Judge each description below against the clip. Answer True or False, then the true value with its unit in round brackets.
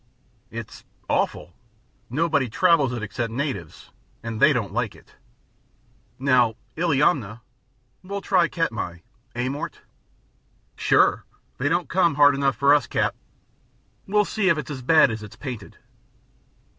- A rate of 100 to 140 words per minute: True (135 wpm)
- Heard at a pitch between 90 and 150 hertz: True (140 Hz)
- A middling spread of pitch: False (5.7 semitones)